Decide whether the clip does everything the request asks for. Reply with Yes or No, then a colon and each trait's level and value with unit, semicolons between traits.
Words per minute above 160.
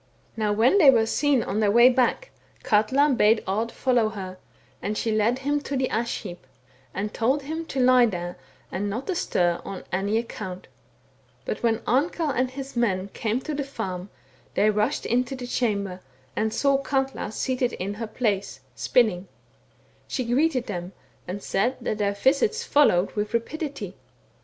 Yes: average, 185 wpm